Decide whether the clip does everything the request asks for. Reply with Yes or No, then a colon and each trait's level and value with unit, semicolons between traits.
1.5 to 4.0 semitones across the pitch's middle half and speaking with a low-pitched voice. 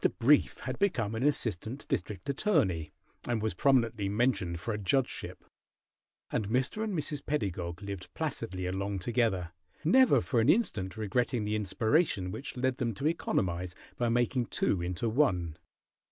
No: wide, 5.6 semitones; low, 115 Hz